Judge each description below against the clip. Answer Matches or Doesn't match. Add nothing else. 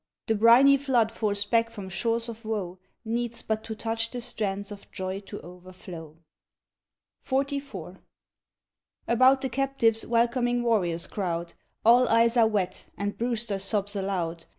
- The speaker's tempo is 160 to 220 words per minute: Doesn't match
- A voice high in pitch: Matches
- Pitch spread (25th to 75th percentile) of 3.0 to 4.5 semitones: Matches